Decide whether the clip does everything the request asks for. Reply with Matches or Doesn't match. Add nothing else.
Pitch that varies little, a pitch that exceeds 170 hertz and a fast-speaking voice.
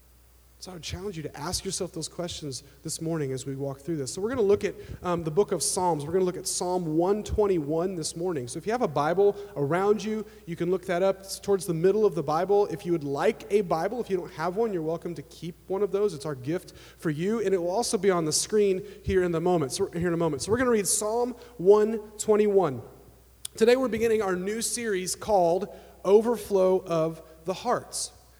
Doesn't match